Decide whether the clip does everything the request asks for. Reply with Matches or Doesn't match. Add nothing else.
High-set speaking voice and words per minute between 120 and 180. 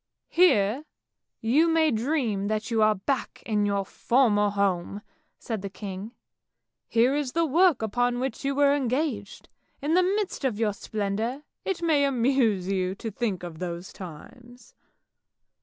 Matches